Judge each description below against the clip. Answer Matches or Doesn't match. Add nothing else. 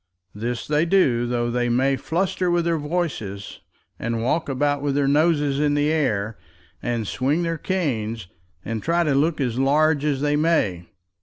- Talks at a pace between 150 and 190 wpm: Matches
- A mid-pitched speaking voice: Matches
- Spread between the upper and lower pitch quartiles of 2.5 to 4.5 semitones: Doesn't match